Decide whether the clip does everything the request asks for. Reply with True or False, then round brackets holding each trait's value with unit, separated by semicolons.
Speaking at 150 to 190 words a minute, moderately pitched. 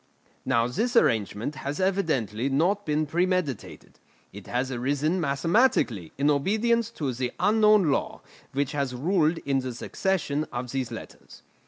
False (140 wpm; 145 Hz)